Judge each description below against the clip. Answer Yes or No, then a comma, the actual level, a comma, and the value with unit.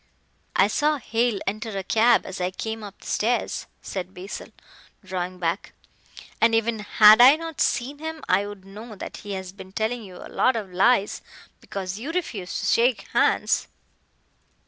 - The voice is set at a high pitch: Yes, high, 215 Hz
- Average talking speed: Yes, average, 170 wpm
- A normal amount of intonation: Yes, average, 4.0 semitones